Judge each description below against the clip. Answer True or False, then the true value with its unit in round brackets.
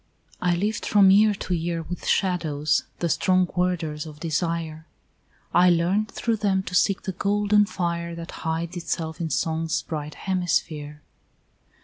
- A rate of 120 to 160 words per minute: True (145 wpm)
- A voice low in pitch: False (175 Hz)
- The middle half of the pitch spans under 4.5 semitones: True (2.8 semitones)